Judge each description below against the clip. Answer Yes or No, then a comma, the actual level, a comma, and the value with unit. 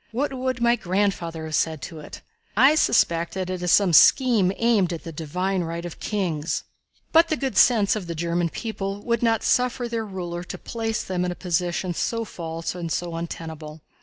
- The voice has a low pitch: No, medium, 185 Hz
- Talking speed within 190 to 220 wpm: Yes, average, 195 wpm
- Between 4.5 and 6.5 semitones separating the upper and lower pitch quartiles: Yes, average, 5.1 semitones